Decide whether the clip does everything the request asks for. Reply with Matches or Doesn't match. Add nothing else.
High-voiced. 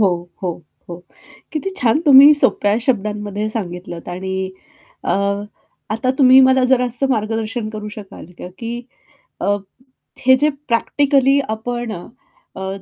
Matches